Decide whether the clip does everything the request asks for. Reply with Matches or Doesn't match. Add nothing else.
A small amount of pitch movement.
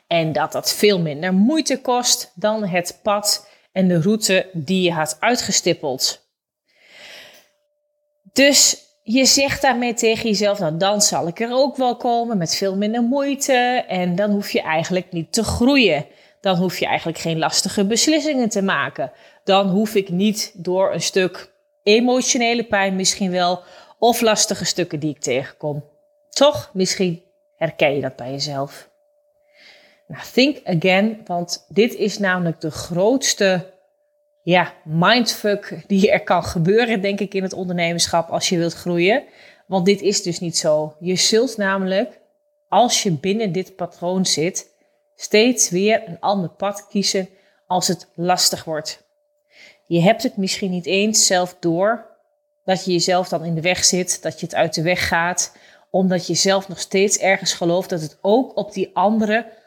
Doesn't match